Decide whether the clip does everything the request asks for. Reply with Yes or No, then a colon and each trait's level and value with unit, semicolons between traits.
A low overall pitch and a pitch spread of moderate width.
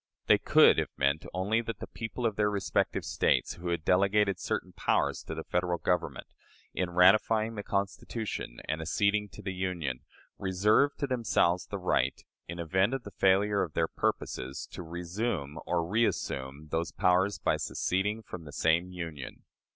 Yes: very low, 90 Hz; average, 3.7 semitones